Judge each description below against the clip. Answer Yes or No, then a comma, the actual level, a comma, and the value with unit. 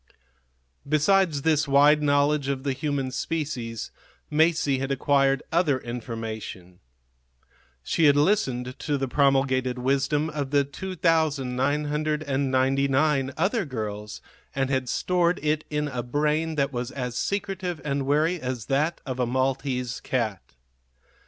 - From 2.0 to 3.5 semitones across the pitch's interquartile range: Yes, average, 2.9 semitones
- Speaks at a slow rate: Yes, slow, 125 wpm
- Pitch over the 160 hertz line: No, medium, 140 Hz